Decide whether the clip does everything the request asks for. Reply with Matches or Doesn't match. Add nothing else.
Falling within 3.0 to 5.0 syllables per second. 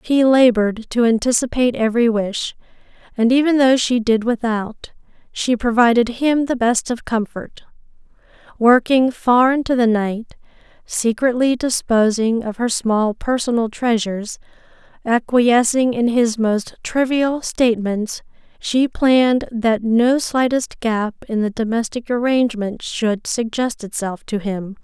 Matches